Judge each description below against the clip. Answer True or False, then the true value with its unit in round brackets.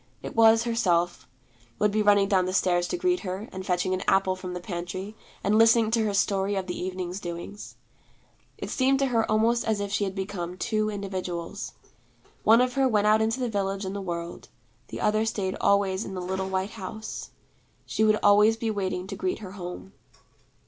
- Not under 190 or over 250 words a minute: True (200 wpm)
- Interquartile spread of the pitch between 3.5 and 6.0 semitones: False (2.8 semitones)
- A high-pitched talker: True (200 Hz)